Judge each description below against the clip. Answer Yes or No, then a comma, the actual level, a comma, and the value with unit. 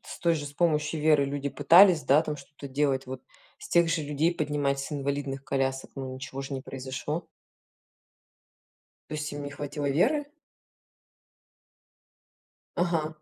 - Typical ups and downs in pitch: No, narrow, 2.3 semitones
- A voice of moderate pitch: Yes, medium, 145 Hz